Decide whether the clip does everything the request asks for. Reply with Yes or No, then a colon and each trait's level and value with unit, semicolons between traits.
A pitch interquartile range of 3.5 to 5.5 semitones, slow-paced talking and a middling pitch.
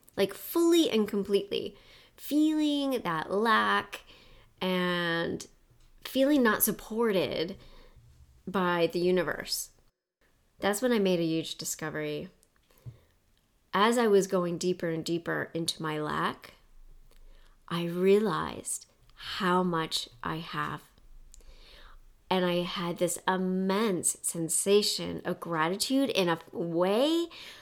Yes: average, 4.2 semitones; slow, 105 wpm; medium, 180 Hz